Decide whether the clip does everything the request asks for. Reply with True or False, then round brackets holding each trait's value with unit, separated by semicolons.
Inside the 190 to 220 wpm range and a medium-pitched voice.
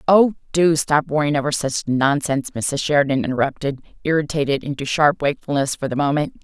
False (160 wpm; 145 Hz)